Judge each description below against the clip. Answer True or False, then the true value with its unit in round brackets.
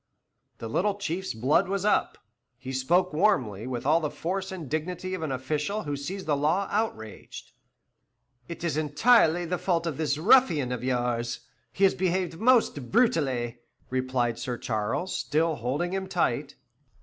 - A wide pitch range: True (6.4 semitones)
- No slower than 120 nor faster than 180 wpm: True (160 wpm)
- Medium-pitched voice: True (155 Hz)